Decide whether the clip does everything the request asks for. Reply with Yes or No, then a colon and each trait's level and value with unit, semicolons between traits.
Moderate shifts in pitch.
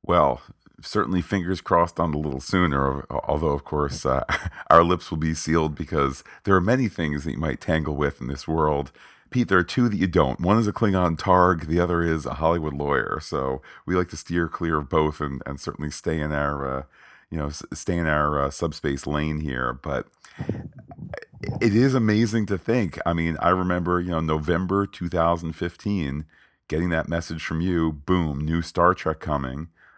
Yes: average, 3.1 semitones